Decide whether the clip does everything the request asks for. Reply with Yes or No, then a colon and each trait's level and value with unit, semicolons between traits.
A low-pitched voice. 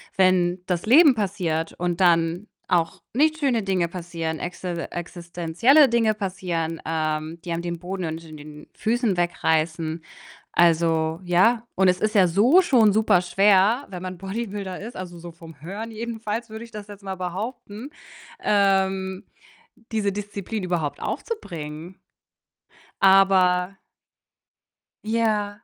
No: medium, 185 Hz